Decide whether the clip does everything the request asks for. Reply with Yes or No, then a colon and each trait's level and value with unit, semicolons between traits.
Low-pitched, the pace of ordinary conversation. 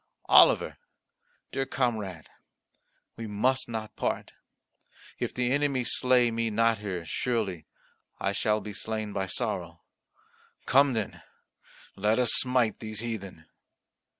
No: low, 110 Hz; slow, 120 wpm